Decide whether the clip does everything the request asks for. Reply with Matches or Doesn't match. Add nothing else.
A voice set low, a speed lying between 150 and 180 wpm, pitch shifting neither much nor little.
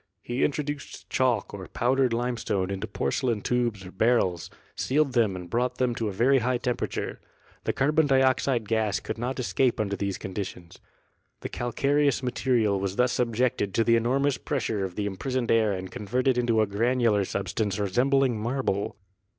Matches